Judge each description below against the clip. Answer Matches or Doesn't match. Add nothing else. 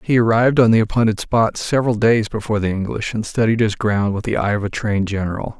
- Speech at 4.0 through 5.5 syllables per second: Doesn't match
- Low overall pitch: Matches